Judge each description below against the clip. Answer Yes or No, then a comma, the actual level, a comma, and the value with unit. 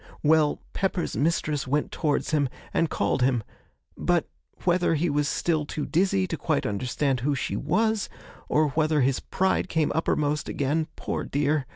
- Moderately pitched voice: Yes, medium, 150 Hz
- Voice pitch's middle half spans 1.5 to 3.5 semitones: Yes, narrow, 2.5 semitones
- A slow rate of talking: No, average, 160 wpm